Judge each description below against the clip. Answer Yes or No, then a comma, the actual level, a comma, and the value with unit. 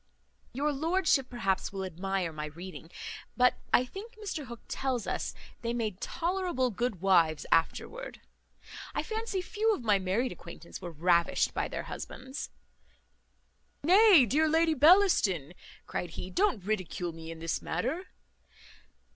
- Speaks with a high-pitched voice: Yes, high, 235 Hz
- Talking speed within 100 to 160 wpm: Yes, average, 140 wpm